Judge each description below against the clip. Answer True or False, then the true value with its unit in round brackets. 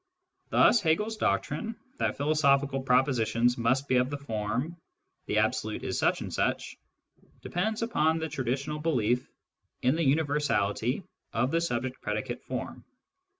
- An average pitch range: True (4.5 semitones)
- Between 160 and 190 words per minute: False (145 wpm)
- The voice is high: False (140 Hz)